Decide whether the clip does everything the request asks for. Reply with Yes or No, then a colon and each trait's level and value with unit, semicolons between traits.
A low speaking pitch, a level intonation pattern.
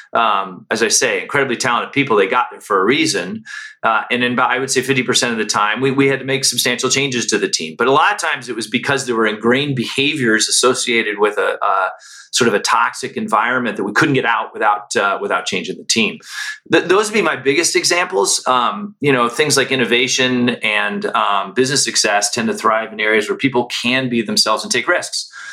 No: low, 130 Hz; average, 4.6 semitones